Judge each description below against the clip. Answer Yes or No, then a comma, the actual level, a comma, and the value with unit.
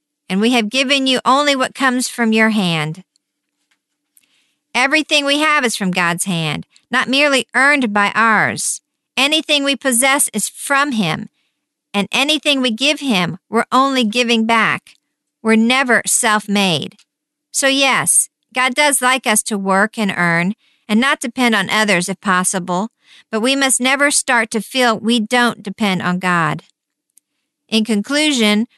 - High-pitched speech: Yes, high, 245 Hz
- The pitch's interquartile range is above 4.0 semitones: Yes, average, 4.7 semitones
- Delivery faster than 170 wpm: No, average, 150 wpm